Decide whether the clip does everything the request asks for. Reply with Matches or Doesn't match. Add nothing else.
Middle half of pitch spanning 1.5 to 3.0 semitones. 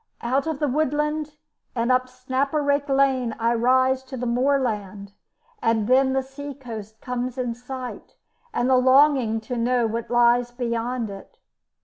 Matches